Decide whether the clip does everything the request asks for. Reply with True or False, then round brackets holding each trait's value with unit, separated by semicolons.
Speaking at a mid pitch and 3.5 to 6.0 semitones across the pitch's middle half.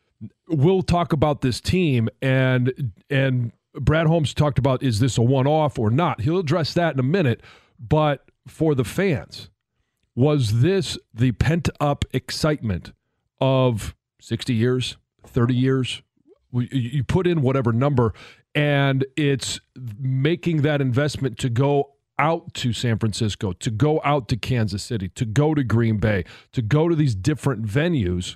False (130 Hz; 4.0 semitones)